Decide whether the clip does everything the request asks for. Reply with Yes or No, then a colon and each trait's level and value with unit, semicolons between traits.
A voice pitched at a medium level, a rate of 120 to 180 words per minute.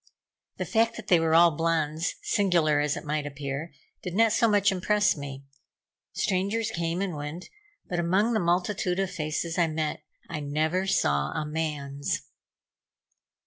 Yes: medium, 165 Hz; average, 155 wpm